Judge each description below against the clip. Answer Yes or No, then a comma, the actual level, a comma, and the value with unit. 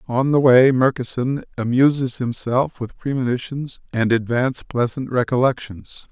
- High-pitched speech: No, low, 125 Hz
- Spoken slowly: Yes, slow, 120 wpm